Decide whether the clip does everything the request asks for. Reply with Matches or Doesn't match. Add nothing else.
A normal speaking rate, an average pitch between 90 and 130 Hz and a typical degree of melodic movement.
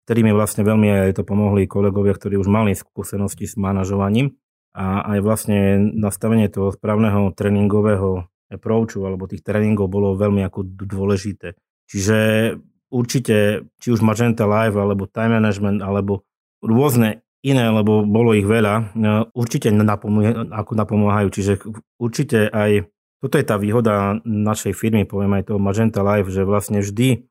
Doesn't match